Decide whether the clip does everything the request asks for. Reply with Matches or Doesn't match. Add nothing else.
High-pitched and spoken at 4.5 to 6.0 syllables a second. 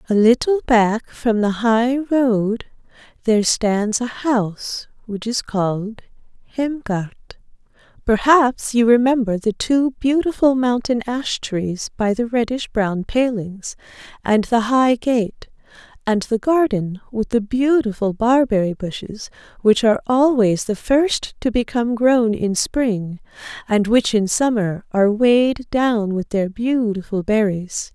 Doesn't match